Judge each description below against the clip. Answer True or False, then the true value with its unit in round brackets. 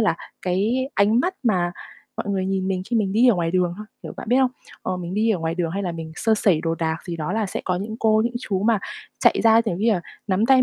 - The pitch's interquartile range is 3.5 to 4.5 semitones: True (3.9 semitones)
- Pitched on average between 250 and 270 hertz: False (195 Hz)